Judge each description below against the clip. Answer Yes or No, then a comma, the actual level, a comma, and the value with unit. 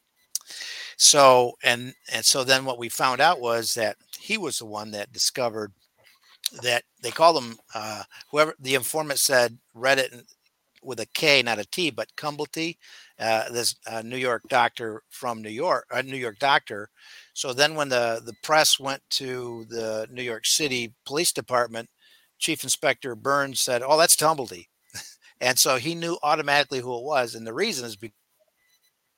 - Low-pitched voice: Yes, low, 125 Hz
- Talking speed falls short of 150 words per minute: No, average, 175 wpm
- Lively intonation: No, average, 3.9 semitones